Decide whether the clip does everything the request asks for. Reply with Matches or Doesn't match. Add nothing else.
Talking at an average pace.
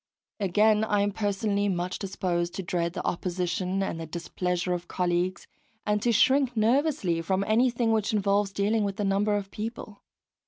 Matches